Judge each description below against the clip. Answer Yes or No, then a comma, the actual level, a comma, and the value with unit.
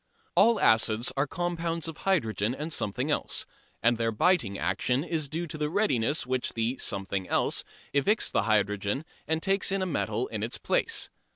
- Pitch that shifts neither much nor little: No, wide, 7.6 semitones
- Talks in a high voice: No, medium, 140 Hz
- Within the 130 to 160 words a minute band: No, average, 180 wpm